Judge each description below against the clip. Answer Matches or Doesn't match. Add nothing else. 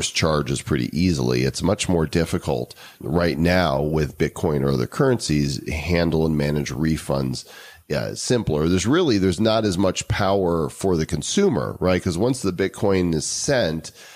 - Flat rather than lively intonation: Doesn't match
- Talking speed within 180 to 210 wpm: Doesn't match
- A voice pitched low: Matches